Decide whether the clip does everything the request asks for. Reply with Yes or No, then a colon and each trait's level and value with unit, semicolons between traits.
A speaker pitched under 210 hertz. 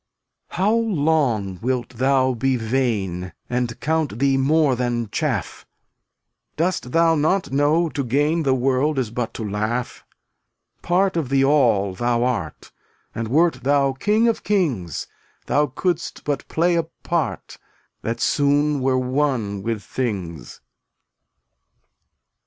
Yes: low, 135 Hz